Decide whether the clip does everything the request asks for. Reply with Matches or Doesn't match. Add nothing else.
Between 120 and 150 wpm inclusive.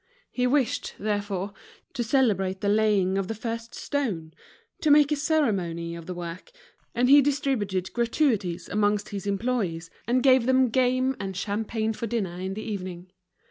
Doesn't match